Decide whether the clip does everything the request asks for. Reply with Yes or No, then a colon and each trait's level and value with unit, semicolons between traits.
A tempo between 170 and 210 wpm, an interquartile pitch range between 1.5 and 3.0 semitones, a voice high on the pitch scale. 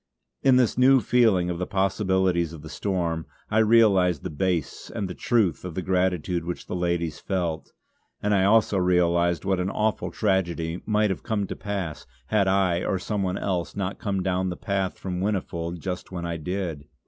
No: average, 190 wpm; narrow, 2.5 semitones; very low, 95 Hz